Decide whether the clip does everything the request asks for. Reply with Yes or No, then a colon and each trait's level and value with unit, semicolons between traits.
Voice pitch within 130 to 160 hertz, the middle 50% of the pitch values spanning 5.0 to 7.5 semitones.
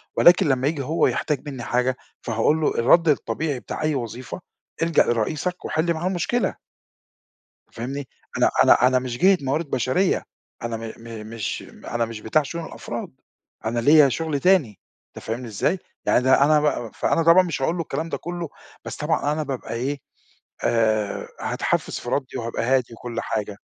Yes: low, 135 Hz; wide, 5.4 semitones